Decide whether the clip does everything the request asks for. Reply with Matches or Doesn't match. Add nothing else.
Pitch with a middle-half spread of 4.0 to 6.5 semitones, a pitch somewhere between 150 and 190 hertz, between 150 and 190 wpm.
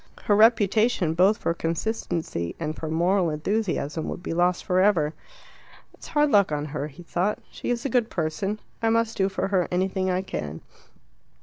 Matches